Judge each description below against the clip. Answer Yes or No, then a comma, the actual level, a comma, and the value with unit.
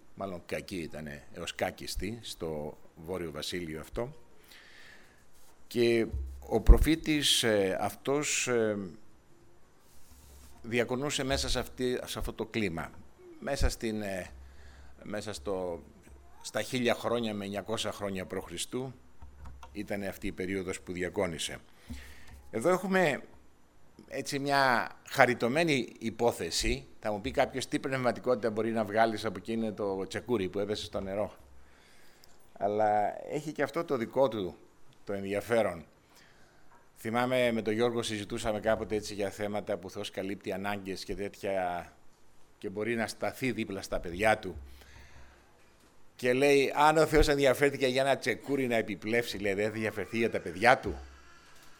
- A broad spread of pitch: No, average, 4.8 semitones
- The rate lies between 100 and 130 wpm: Yes, average, 125 wpm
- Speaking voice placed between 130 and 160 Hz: No, low, 105 Hz